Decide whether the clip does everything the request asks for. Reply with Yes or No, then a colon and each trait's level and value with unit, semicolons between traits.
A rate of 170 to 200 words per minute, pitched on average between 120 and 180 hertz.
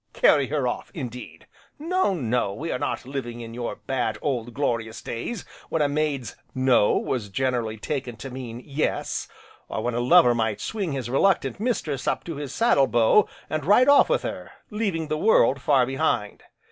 Yes: average, 180 wpm; low, 135 Hz